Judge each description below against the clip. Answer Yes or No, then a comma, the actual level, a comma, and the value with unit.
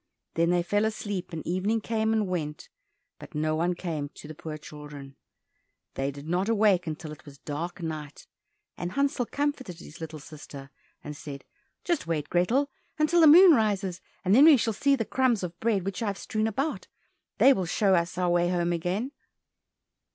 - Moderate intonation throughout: No, wide, 5.9 semitones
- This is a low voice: No, medium, 180 Hz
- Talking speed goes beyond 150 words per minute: Yes, average, 190 wpm